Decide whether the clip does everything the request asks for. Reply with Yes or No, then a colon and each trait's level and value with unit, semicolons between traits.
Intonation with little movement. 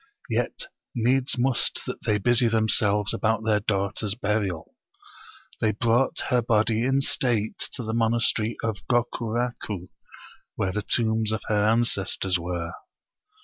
Yes: narrow, 2.3 semitones